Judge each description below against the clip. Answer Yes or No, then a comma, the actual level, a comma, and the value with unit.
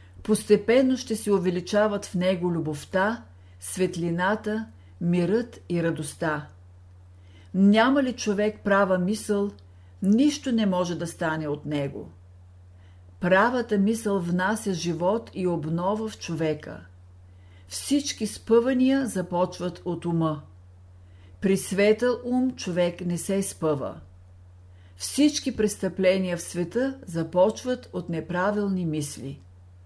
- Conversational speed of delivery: No, slow, 100 wpm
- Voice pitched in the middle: Yes, medium, 180 Hz